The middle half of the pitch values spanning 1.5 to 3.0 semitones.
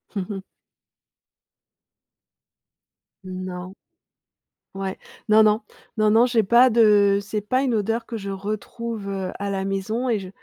Yes: narrow, 2.6 semitones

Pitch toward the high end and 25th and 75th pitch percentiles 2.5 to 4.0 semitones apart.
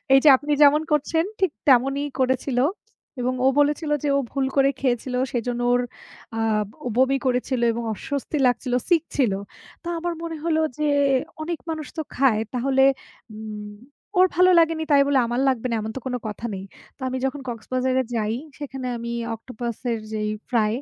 Yes: very high, 260 Hz; average, 3.6 semitones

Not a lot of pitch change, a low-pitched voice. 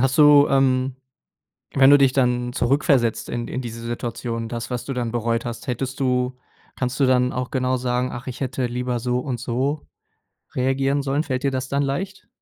Yes: narrow, 1.8 semitones; low, 125 Hz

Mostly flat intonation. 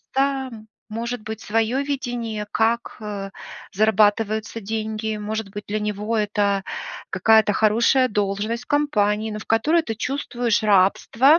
Yes: narrow, 2.1 semitones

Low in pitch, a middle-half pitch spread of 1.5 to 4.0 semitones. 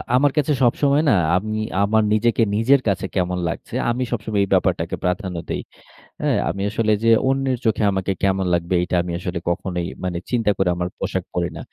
No: low, 100 Hz; average, 4.6 semitones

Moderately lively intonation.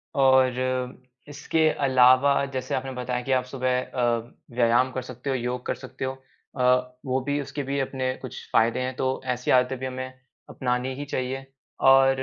No: narrow, 0.9 semitones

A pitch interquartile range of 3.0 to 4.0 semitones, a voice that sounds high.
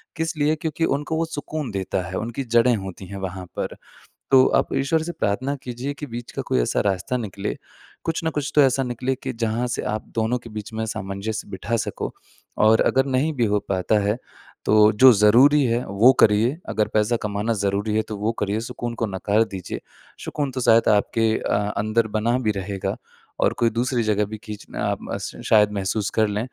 No: average, 3.7 semitones; low, 110 Hz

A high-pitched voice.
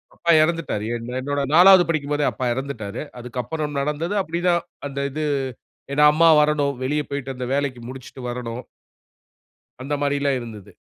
No: medium, 140 Hz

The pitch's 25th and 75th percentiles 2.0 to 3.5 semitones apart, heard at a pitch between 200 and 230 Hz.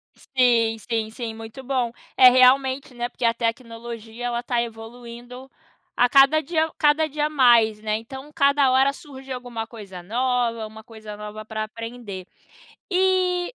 No: average, 3.1 semitones; high, 240 Hz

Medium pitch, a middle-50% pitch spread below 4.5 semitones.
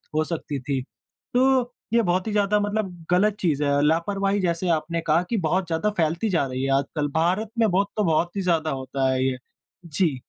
No: medium, 170 Hz; average, 4.9 semitones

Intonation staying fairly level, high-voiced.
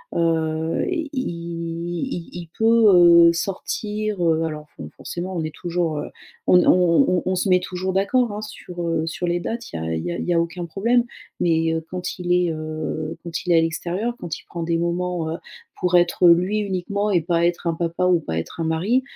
No: narrow, 2.1 semitones; medium, 175 Hz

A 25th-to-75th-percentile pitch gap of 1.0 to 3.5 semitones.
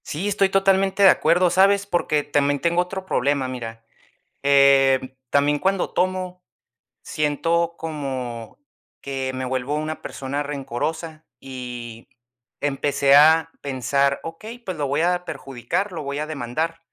No: average, 4.6 semitones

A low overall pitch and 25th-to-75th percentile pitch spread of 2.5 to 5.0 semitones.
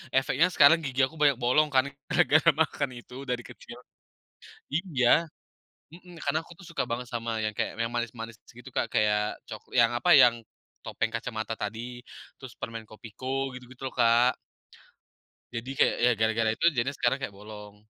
Yes: low, 125 Hz; average, 3.6 semitones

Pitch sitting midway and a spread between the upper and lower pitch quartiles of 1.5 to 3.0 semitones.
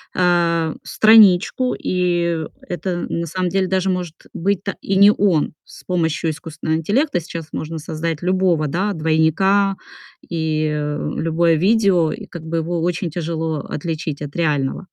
Yes: medium, 170 Hz; average, 2.7 semitones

